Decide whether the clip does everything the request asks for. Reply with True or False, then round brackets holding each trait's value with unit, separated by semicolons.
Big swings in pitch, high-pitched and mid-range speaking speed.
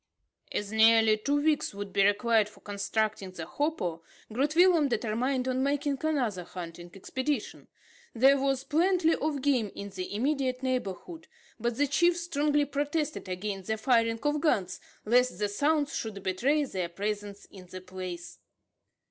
True (6.2 semitones; 240 Hz; 150 wpm)